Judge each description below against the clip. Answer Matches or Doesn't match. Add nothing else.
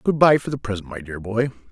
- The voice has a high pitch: Doesn't match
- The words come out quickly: Matches